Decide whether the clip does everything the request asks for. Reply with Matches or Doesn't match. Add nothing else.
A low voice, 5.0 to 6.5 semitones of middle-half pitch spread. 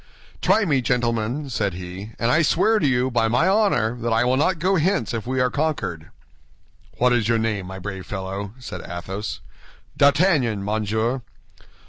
Matches